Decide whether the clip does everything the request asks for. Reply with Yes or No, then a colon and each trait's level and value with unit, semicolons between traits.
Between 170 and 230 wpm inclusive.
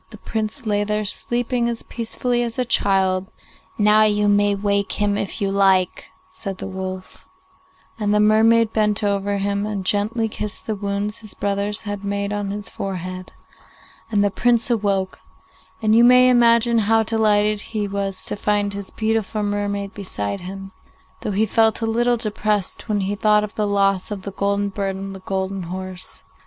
Yes: average, 175 wpm